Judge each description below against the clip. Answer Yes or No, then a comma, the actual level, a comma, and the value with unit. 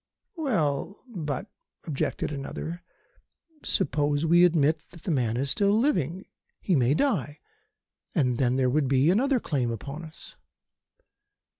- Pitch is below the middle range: No, medium, 150 Hz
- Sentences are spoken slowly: Yes, slow, 130 wpm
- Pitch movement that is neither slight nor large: Yes, average, 4.7 semitones